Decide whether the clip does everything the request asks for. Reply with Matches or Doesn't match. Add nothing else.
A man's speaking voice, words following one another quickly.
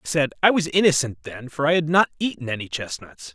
Matches